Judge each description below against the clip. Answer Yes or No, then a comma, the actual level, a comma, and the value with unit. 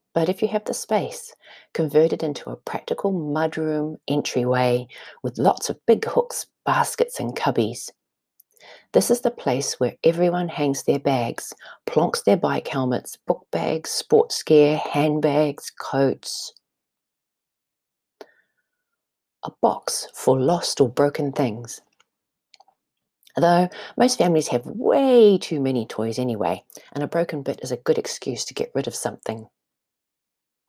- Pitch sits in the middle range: Yes, medium, 155 Hz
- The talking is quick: No, slow, 135 wpm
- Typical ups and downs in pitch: No, wide, 7.1 semitones